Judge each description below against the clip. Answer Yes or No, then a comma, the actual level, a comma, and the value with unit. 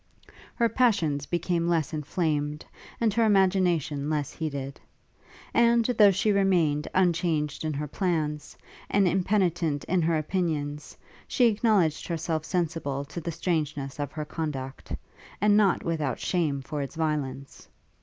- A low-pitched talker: No, medium, 160 Hz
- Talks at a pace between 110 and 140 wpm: Yes, slow, 135 wpm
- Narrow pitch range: No, average, 3.9 semitones